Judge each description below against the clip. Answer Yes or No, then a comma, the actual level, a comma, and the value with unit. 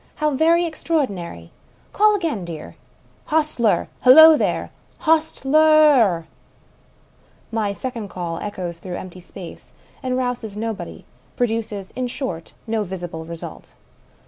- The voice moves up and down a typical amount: No, wide, 8.7 semitones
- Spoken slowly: Yes, slow, 130 wpm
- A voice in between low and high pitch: No, high, 225 Hz